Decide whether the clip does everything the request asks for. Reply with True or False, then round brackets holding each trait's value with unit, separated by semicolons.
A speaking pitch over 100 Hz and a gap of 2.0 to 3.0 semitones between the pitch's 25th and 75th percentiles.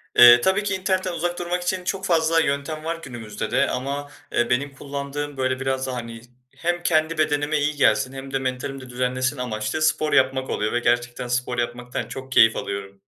False (135 Hz; 4.1 semitones)